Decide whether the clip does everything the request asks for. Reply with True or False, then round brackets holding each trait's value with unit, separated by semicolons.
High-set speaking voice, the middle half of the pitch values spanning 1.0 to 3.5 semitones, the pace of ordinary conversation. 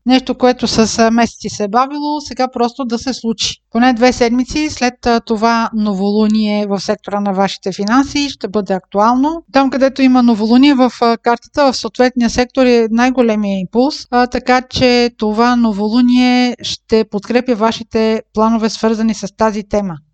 True (235 Hz; 2.5 semitones; 150 wpm)